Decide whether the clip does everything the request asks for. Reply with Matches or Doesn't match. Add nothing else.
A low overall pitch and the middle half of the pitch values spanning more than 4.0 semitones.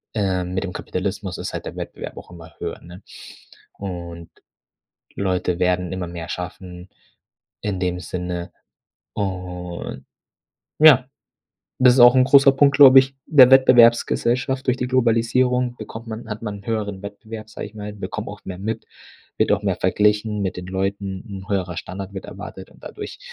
Matches